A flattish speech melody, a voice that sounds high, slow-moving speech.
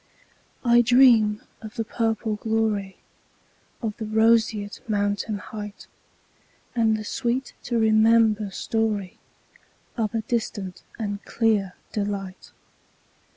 Yes: narrow, 1.7 semitones; high, 220 Hz; slow, 90 wpm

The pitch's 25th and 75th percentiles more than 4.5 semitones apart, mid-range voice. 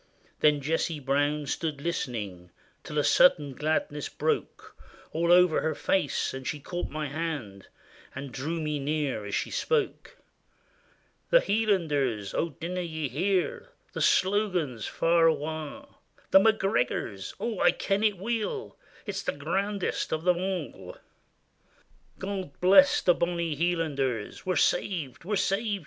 Yes: average, 4.9 semitones; medium, 165 Hz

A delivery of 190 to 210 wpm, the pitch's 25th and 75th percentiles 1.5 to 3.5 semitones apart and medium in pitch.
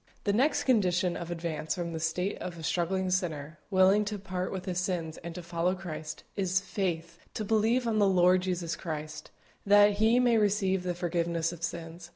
Yes: average, 195 wpm; average, 2.9 semitones; medium, 180 Hz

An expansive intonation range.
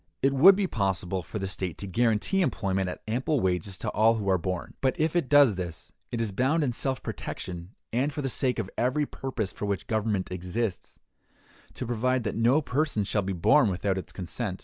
Yes: wide, 5.7 semitones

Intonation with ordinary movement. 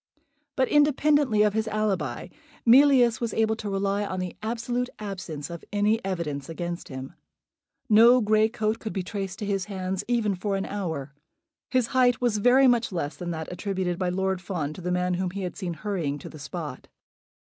Yes: average, 3.9 semitones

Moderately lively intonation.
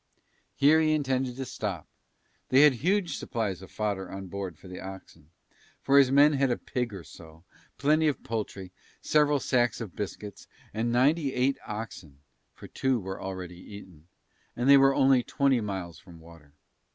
No: wide, 6.3 semitones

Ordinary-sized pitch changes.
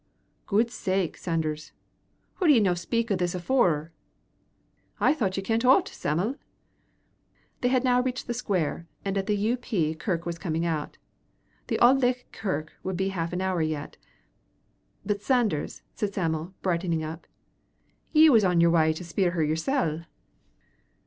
No: wide, 5.9 semitones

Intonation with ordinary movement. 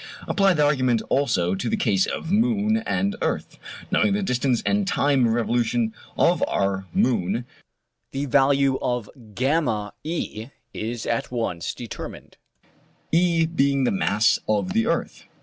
No: wide, 6.6 semitones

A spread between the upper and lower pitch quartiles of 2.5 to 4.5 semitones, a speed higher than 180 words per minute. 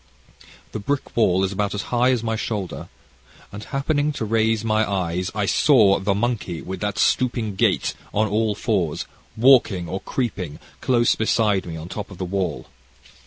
No: average, 3.5 semitones; average, 170 wpm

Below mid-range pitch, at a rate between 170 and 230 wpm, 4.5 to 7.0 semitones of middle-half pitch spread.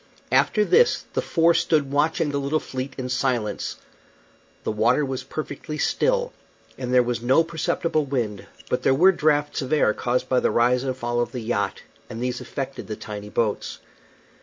No: low, 130 Hz; average, 180 wpm; average, 4.0 semitones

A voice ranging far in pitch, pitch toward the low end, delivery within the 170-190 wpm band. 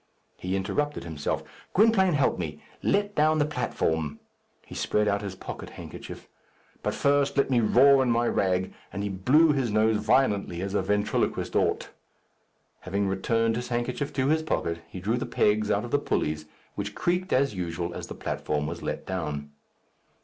Yes: wide, 6.9 semitones; low, 110 Hz; average, 175 wpm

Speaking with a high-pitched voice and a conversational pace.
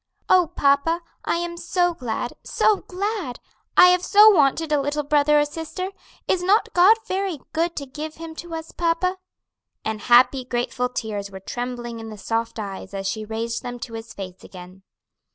Yes: very high, 285 Hz; average, 180 wpm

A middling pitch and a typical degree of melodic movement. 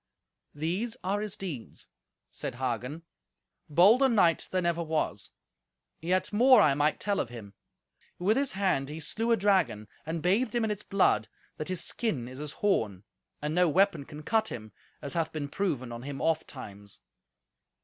No: medium, 165 Hz; wide, 6.6 semitones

